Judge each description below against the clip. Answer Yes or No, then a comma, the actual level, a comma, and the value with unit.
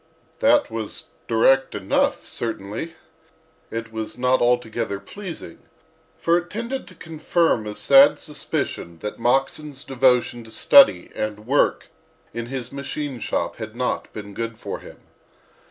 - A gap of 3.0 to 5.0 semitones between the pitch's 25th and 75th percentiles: No, wide, 5.5 semitones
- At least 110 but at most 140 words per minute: Yes, slow, 135 wpm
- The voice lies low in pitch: Yes, low, 125 Hz